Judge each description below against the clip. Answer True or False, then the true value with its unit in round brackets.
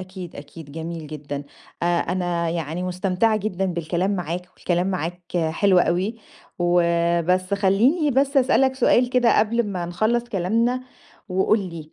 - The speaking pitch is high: False (180 Hz)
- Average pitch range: True (4.1 semitones)